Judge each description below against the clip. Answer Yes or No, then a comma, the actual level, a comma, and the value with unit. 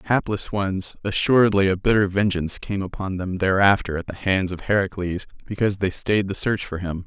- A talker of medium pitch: No, very low, 95 Hz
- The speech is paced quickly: No, average, 185 wpm